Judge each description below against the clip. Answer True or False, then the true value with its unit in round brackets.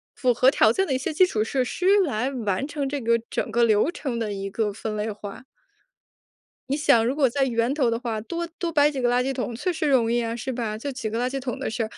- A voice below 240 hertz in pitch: False (245 Hz)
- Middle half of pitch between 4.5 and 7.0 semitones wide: False (3.5 semitones)